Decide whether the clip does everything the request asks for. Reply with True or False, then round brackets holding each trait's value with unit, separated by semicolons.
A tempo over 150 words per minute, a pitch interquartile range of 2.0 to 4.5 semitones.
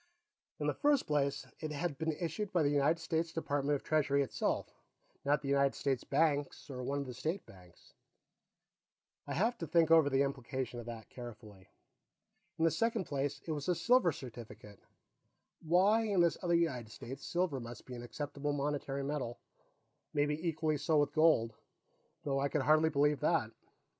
True (175 wpm; 3.2 semitones)